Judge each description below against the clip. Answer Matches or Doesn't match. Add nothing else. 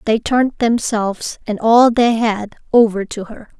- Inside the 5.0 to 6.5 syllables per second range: Doesn't match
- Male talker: Doesn't match